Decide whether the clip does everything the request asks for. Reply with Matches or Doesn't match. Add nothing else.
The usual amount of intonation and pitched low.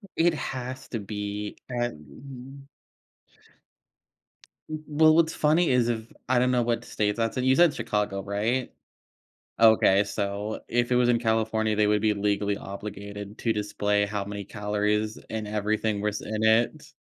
Matches